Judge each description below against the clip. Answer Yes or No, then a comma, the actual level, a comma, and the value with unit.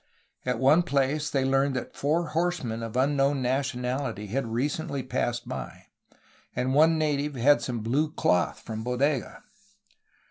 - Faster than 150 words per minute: No, average, 145 wpm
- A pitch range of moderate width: Yes, average, 3.2 semitones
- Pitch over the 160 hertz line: No, low, 135 Hz